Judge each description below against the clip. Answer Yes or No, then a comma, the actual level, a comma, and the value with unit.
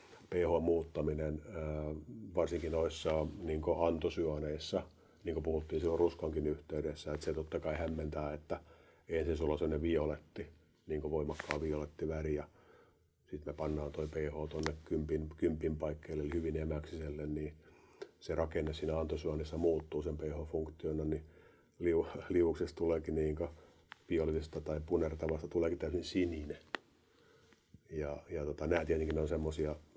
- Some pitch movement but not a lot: No, narrow, 1.0 semitones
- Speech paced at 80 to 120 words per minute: No, average, 130 wpm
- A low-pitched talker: Yes, very low, 80 Hz